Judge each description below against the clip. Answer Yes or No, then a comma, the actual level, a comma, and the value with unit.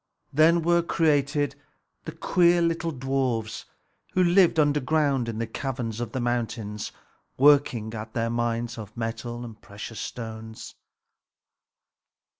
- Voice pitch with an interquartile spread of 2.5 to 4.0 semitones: No, average, 4.7 semitones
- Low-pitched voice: Yes, low, 120 Hz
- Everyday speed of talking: No, slow, 120 wpm